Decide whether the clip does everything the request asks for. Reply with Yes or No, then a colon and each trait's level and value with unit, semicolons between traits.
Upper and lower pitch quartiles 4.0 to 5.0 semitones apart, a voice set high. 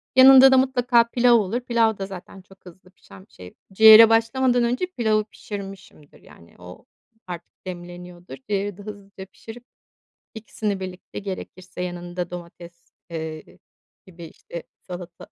Yes: average, 4.4 semitones; high, 195 Hz